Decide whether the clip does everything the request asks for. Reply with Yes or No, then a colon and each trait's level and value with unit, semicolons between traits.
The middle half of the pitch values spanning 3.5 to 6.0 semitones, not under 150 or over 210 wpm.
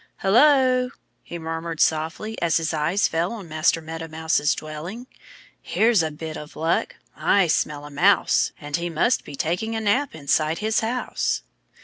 Yes: wide, 5.4 semitones; average, 160 wpm